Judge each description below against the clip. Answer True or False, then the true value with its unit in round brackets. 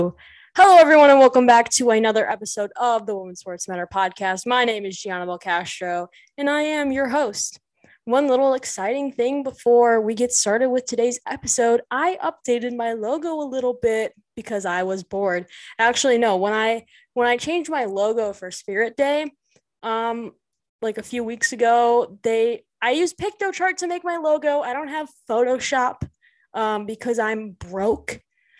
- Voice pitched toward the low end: False (240 Hz)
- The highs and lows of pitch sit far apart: False (4.8 semitones)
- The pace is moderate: True (170 wpm)